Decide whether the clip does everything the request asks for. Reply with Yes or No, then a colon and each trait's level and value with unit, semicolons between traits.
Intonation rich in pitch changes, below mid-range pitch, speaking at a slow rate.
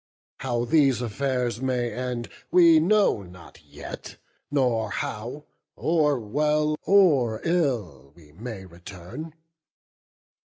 Yes: wide, 6.0 semitones; low, 125 Hz; slow, 105 wpm